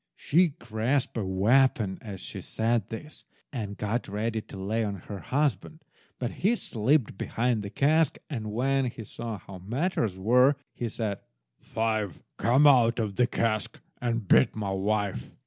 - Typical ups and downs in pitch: Yes, average, 3.8 semitones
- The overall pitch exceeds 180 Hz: No, low, 115 Hz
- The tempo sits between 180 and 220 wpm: No, average, 160 wpm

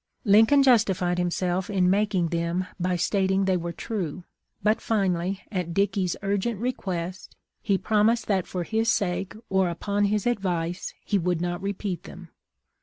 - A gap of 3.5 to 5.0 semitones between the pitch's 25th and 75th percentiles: No, narrow, 2.6 semitones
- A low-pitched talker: No, high, 190 Hz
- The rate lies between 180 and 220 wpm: No, average, 160 wpm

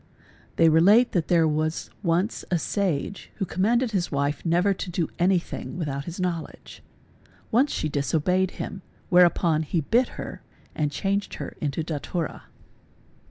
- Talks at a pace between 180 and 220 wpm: No, average, 155 wpm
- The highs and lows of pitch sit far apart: No, average, 3.6 semitones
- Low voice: No, medium, 175 Hz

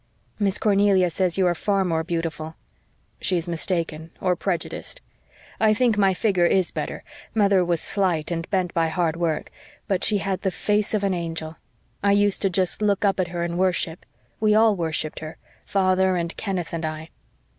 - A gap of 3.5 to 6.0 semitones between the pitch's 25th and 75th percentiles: No, average, 3.0 semitones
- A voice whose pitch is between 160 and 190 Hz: Yes, medium, 185 Hz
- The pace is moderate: Yes, average, 185 wpm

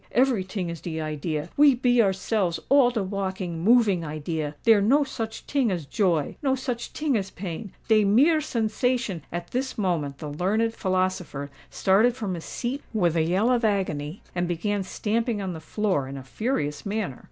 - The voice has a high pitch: Yes, high, 195 Hz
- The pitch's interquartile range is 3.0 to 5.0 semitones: No, wide, 5.6 semitones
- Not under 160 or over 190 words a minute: Yes, average, 170 wpm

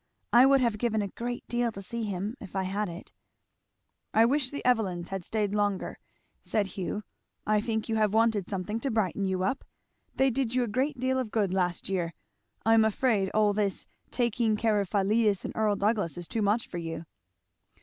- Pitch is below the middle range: No, high, 215 Hz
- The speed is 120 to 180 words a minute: No, average, 200 wpm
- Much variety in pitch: No, average, 3.2 semitones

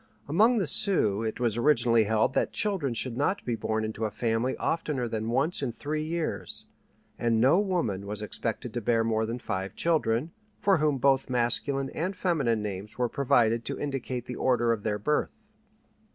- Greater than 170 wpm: Yes, average, 180 wpm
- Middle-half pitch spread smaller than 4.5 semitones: No, average, 4.9 semitones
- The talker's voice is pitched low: Yes, low, 120 Hz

